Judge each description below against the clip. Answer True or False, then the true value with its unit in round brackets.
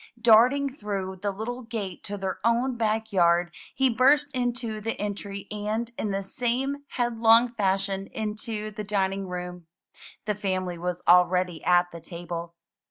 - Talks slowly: False (150 wpm)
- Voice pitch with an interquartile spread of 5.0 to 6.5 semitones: False (3.9 semitones)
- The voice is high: True (210 Hz)